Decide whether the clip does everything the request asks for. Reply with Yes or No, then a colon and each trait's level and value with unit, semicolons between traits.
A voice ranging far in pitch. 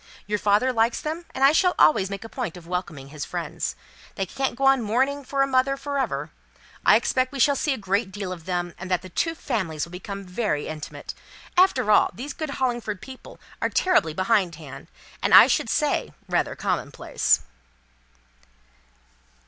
Yes: wide, 6.9 semitones